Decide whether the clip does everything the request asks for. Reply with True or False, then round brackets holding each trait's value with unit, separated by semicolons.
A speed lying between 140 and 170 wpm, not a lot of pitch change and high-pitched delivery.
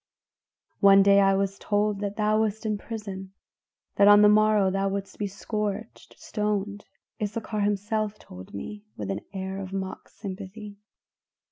True (150 wpm; 1.4 semitones; 205 Hz)